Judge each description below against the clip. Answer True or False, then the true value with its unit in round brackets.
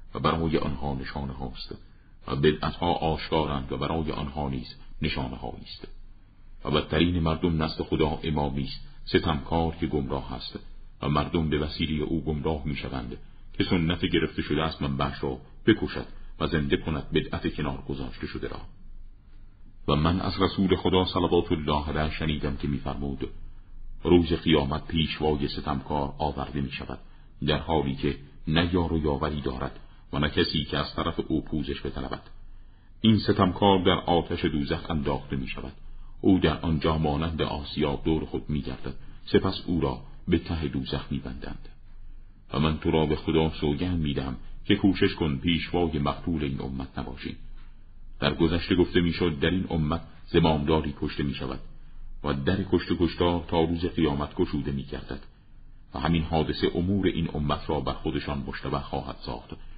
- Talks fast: True (160 wpm)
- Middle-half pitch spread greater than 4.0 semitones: False (3.3 semitones)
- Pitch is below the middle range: True (80 Hz)